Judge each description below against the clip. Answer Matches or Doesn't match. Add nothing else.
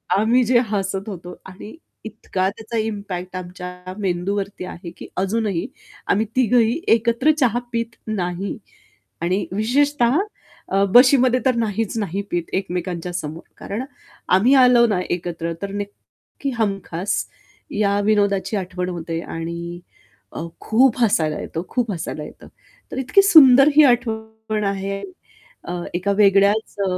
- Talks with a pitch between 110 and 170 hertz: Doesn't match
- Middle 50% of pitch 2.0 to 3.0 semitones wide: Doesn't match